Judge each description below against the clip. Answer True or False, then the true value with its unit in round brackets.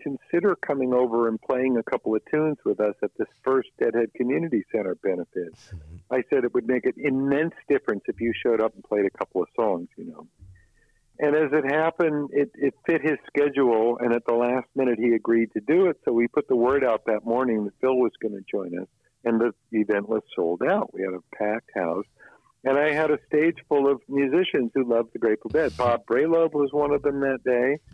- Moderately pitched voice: False (125 Hz)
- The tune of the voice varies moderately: True (3.9 semitones)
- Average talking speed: False (225 wpm)